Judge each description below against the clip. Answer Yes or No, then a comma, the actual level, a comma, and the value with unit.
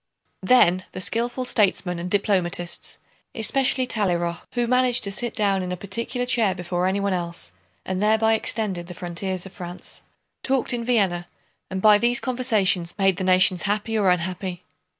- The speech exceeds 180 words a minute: No, average, 160 wpm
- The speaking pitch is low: No, high, 195 Hz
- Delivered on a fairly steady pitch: No, average, 4.0 semitones